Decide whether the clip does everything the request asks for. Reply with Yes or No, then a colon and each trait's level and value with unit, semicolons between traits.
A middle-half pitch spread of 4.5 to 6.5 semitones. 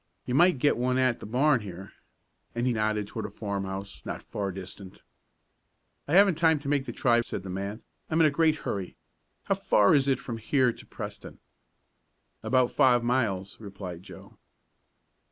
Yes: average, 5.2 semitones